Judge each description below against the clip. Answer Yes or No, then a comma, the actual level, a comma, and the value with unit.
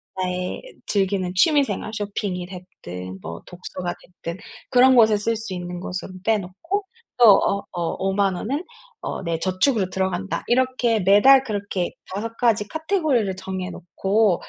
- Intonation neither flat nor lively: Yes, average, 3.9 semitones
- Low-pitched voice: No, high, 195 Hz